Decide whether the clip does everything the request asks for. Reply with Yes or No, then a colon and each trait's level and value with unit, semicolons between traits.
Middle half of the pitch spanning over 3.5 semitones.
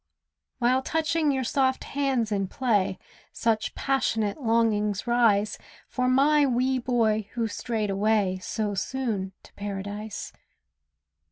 Yes: average, 4.0 semitones